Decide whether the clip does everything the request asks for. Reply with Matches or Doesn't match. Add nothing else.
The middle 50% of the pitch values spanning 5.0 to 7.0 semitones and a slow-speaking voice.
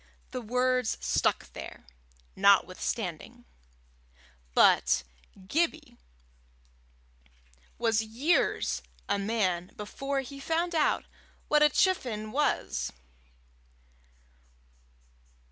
Matches